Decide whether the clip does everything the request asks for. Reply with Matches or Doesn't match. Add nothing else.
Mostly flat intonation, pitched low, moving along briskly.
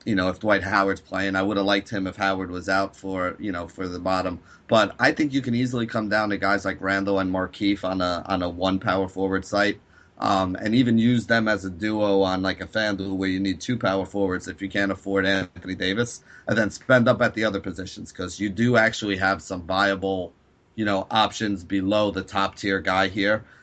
Matches